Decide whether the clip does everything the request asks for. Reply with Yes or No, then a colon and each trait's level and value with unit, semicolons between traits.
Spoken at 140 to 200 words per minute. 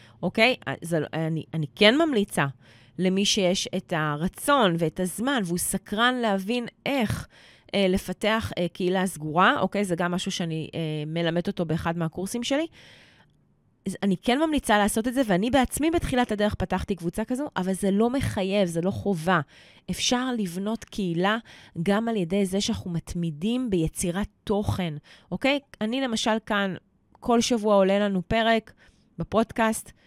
Yes: average, 145 wpm